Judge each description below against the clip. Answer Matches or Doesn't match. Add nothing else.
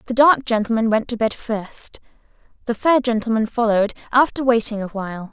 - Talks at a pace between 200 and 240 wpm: Doesn't match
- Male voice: Doesn't match